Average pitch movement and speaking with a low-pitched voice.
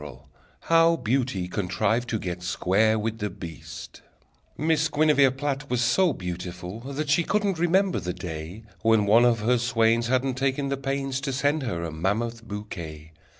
No: wide, 6.5 semitones; low, 115 Hz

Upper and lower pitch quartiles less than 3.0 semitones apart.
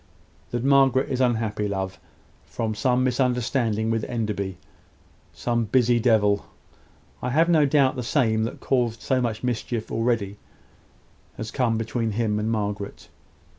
Yes: narrow, 2.6 semitones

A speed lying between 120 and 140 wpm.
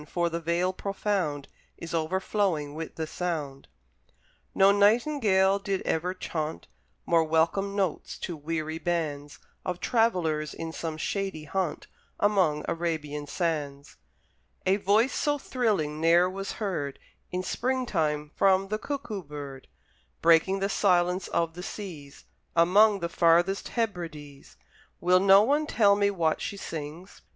Yes: slow, 135 wpm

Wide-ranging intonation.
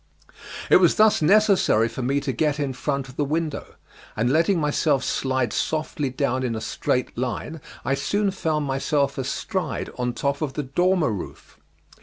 No: average, 3.4 semitones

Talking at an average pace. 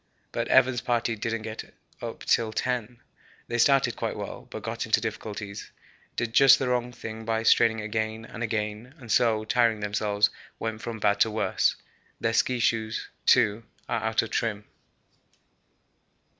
Yes: average, 155 wpm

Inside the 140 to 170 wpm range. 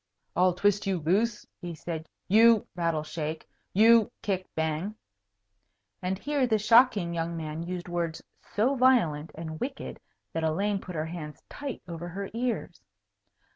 Yes: average, 150 wpm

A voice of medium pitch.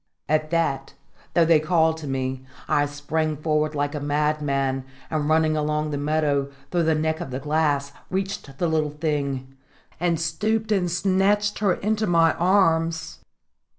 Yes: medium, 155 Hz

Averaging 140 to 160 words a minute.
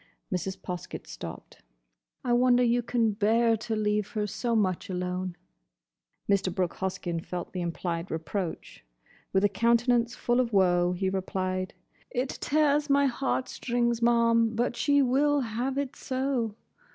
Yes: average, 145 wpm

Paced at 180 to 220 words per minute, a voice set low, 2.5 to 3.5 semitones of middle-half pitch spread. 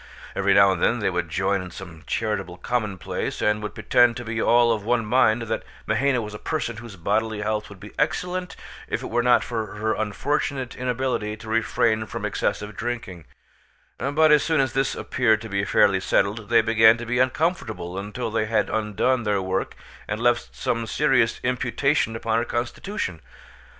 Yes: average, 185 wpm; low, 110 Hz; average, 2.9 semitones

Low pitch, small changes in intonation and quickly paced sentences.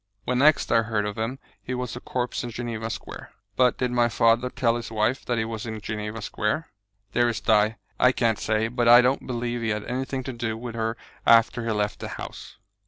Yes: low, 115 Hz; narrow, 1.8 semitones; fast, 220 wpm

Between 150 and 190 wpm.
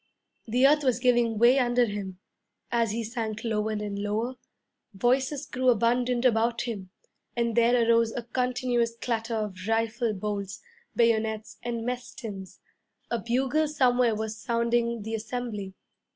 No: average, 140 wpm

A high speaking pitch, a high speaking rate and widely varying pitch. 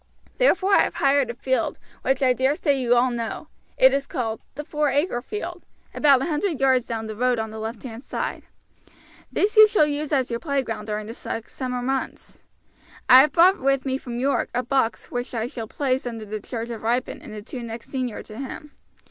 No: very high, 255 Hz; fast, 215 wpm; average, 3.3 semitones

